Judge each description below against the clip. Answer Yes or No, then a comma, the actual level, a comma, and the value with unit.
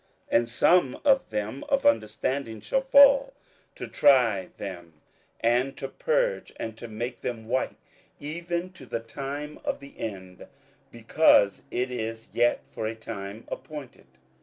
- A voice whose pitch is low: Yes, low, 125 Hz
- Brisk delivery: No, average, 145 wpm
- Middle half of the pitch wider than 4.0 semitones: Yes, wide, 5.4 semitones